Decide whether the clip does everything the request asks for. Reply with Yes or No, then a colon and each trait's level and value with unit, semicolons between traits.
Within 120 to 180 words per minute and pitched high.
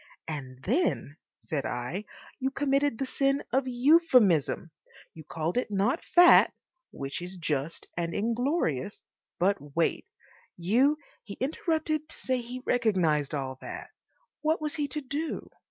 Yes: average, 140 wpm; high, 230 Hz